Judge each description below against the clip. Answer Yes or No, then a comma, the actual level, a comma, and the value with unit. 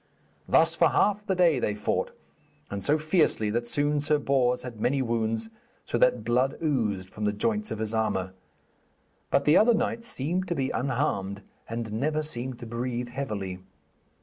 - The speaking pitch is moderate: No, low, 125 Hz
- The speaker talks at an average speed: Yes, average, 175 wpm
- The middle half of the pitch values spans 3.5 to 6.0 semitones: Yes, average, 5.3 semitones